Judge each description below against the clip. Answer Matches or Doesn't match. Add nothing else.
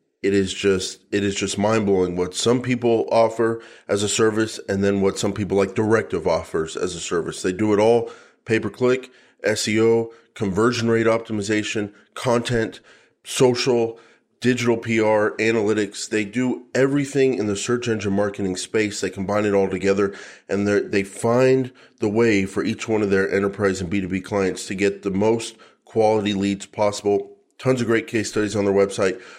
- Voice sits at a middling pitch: Doesn't match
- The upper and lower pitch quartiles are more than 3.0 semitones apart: Doesn't match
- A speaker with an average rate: Matches